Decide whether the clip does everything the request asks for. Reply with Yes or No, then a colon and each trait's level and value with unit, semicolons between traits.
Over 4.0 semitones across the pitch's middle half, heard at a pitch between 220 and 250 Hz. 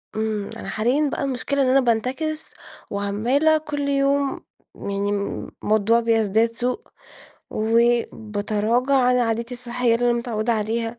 No: average, 3.4 semitones; high, 235 Hz